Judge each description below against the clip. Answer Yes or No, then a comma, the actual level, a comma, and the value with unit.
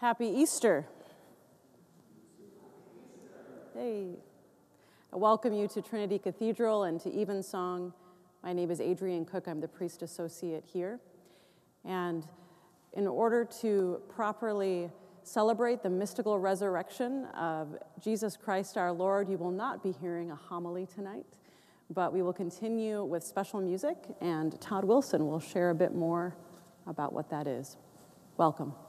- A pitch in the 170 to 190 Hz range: Yes, medium, 185 Hz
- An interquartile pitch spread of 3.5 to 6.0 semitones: No, average, 3.1 semitones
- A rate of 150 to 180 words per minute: No, slow, 135 wpm